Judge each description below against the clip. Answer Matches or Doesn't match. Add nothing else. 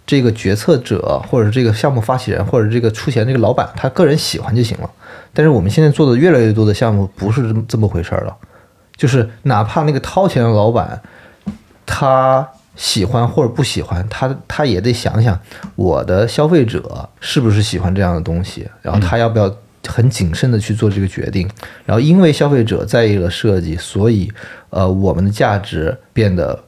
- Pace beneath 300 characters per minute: Doesn't match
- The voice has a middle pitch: Doesn't match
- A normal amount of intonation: Matches